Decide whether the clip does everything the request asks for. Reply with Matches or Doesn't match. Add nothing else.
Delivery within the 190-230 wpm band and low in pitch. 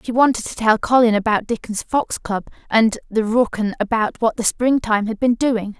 Doesn't match